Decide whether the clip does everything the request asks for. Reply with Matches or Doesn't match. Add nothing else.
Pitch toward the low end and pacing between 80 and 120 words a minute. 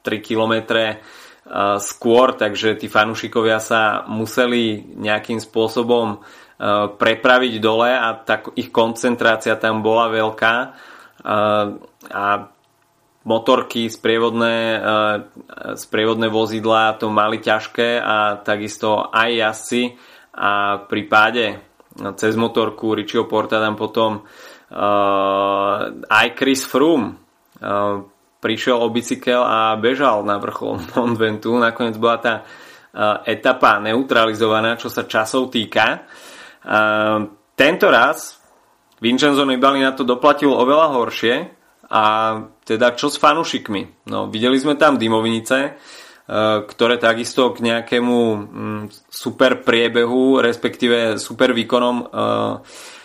Matches